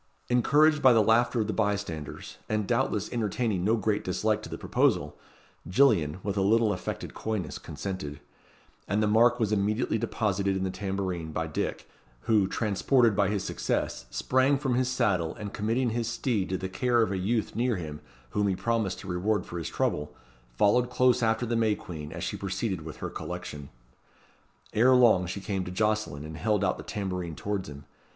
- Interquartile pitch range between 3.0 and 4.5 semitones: Yes, average, 3.8 semitones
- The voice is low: Yes, low, 105 Hz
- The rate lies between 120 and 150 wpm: No, average, 190 wpm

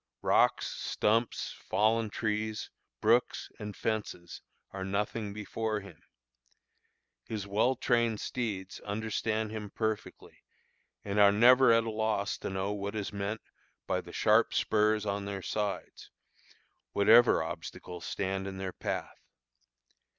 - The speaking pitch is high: No, low, 105 Hz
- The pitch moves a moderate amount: No, narrow, 1.8 semitones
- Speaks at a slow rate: Yes, slow, 125 wpm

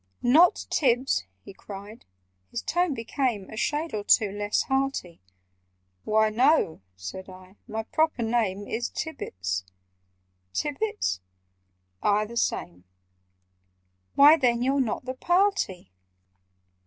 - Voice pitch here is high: Yes, high, 220 Hz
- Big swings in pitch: Yes, wide, 6.3 semitones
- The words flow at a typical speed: No, slow, 110 wpm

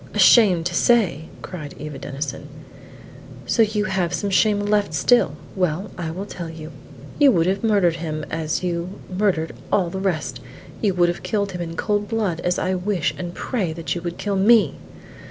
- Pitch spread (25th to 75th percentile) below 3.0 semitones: No, average, 3.7 semitones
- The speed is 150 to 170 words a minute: No, average, 185 wpm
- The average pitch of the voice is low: No, medium, 180 Hz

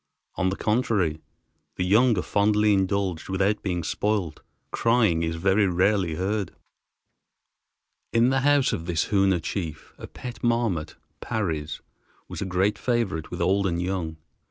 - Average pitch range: Yes, average, 3.6 semitones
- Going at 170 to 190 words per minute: No, average, 145 wpm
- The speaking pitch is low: Yes, very low, 95 Hz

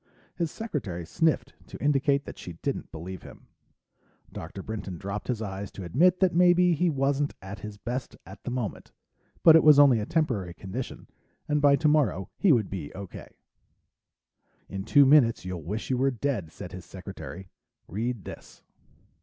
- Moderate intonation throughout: No, wide, 7.3 semitones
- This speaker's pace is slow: No, average, 170 wpm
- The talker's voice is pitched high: No, low, 120 Hz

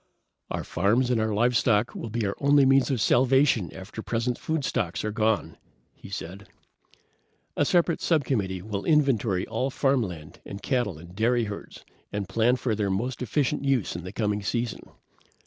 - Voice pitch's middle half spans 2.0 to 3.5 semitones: No, average, 4.6 semitones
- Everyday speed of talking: Yes, average, 165 wpm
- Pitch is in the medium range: No, low, 115 Hz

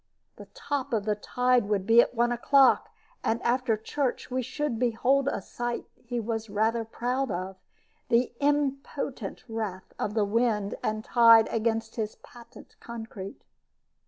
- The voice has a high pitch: Yes, high, 235 Hz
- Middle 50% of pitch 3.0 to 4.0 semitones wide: No, narrow, 2.5 semitones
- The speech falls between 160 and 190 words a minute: No, average, 150 wpm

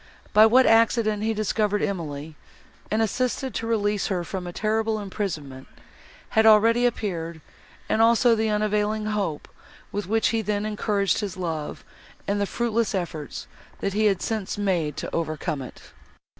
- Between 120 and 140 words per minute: No, average, 155 wpm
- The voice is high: Yes, high, 210 Hz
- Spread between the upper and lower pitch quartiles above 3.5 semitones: No, average, 3.2 semitones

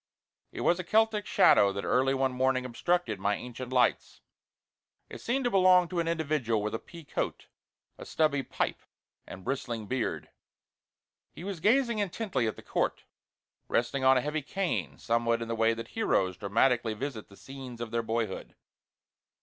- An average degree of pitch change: No, wide, 6.8 semitones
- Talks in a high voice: No, low, 130 Hz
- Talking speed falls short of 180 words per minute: Yes, average, 170 wpm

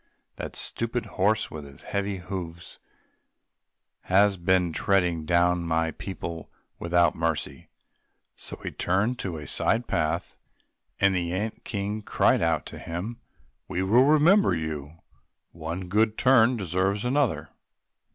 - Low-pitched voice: Yes, very low, 95 Hz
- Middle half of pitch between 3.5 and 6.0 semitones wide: Yes, average, 4.2 semitones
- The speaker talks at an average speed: No, slow, 130 wpm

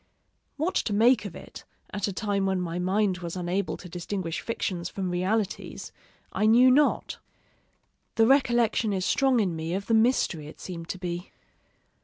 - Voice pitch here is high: Yes, high, 195 Hz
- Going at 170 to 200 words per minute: Yes, average, 175 wpm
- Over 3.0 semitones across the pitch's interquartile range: Yes, average, 4.1 semitones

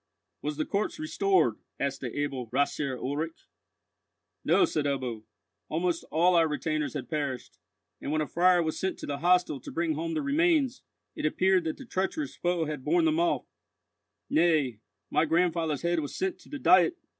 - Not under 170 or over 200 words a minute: Yes, average, 175 wpm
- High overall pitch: No, medium, 160 Hz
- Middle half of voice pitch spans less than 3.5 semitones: No, average, 4.0 semitones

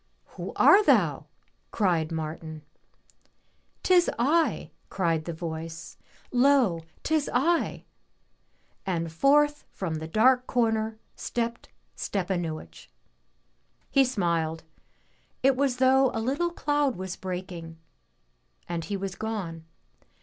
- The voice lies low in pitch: No, high, 200 Hz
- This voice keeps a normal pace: No, slow, 120 wpm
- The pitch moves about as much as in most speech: No, wide, 8.1 semitones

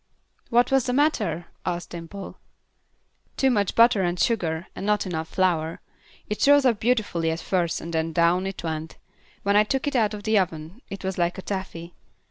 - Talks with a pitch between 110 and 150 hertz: No, high, 190 Hz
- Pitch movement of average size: Yes, average, 4.5 semitones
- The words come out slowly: No, average, 185 wpm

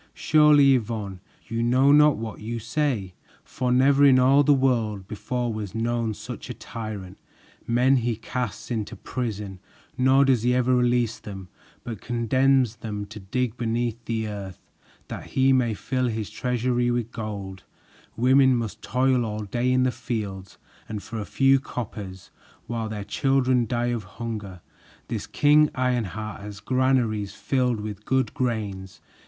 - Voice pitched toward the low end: Yes, low, 120 Hz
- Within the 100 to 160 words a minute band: Yes, average, 155 wpm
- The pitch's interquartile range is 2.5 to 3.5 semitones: Yes, average, 3.2 semitones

